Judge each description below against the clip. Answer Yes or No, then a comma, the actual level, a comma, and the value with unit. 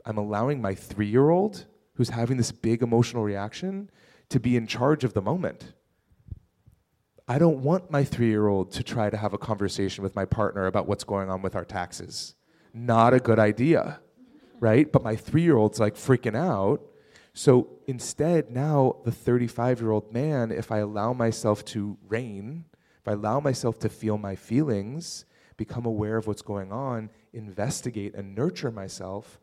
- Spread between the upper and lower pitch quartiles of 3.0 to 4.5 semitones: Yes, average, 3.9 semitones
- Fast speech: No, average, 175 wpm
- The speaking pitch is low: Yes, low, 115 Hz